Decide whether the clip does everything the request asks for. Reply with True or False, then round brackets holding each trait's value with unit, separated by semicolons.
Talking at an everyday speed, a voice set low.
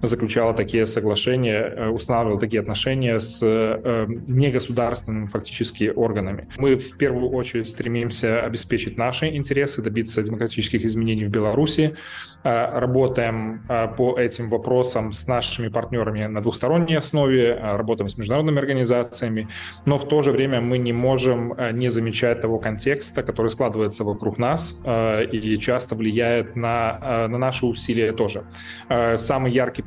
True (125 wpm; 115 Hz)